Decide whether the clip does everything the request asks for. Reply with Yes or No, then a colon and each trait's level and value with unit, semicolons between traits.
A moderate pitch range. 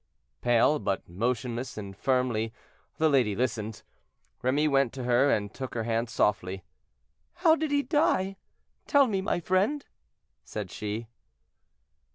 No: wide, 6.8 semitones